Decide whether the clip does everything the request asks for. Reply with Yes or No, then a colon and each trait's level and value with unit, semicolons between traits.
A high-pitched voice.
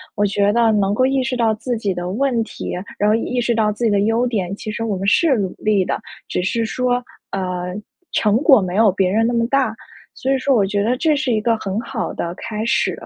Yes: high, 220 Hz